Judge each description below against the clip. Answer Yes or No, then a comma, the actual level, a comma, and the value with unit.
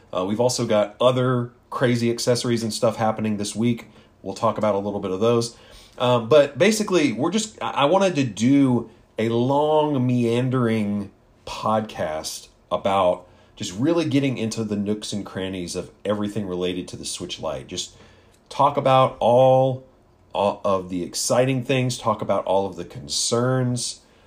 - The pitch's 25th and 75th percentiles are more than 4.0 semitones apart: No, average, 3.7 semitones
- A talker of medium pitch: No, low, 115 Hz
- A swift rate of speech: No, average, 160 wpm